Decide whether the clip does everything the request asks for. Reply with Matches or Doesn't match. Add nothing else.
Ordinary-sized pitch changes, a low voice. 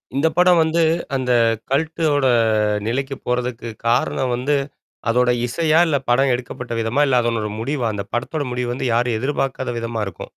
Matches